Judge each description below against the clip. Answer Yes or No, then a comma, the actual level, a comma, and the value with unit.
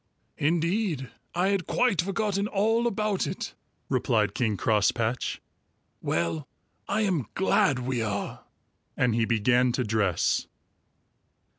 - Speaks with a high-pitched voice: No, low, 130 Hz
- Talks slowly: Yes, slow, 115 wpm